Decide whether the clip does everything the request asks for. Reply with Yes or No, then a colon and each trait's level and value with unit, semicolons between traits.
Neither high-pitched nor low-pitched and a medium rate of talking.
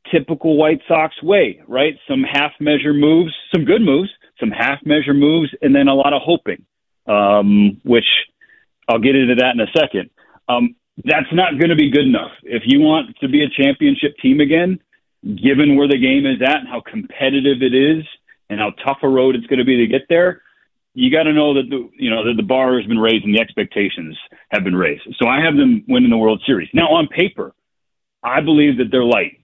No: medium, 150 Hz; fast, 220 wpm